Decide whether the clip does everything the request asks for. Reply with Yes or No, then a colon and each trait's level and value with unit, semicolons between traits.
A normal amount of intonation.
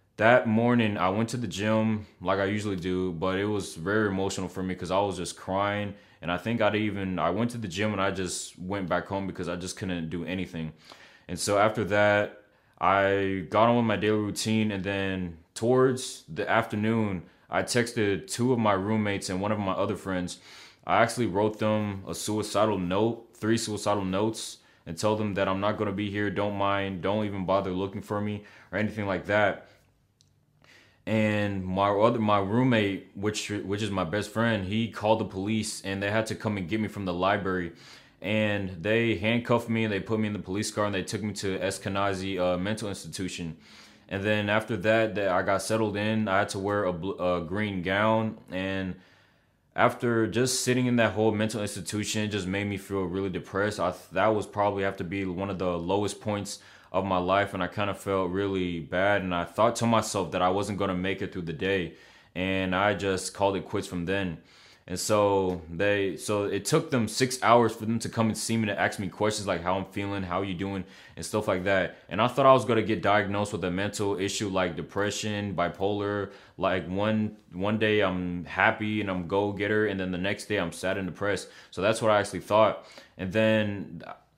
No: narrow, 2.2 semitones